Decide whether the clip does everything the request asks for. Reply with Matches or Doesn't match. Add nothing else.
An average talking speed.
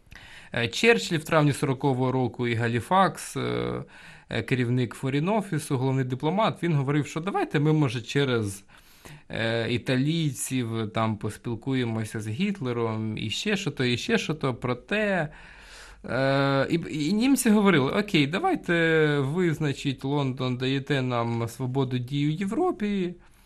Matches